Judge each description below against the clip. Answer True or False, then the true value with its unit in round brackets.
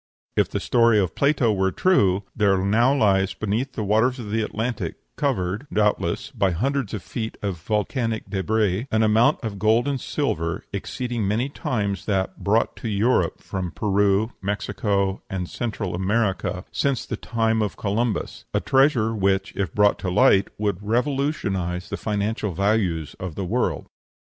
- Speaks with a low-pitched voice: True (105 Hz)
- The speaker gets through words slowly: False (160 wpm)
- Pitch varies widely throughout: False (3.3 semitones)